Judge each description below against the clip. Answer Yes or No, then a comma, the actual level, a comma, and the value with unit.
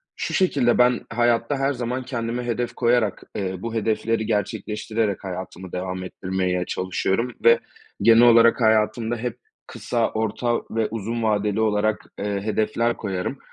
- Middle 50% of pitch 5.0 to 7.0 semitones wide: No, narrow, 2.6 semitones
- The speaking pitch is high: No, low, 110 Hz